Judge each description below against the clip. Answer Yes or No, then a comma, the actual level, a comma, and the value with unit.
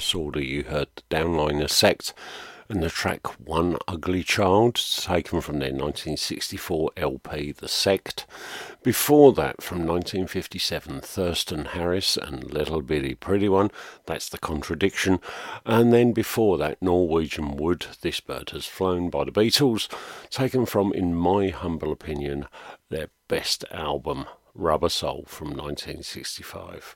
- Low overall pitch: Yes, very low, 90 Hz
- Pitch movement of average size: Yes, average, 4.8 semitones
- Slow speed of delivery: Yes, slow, 130 wpm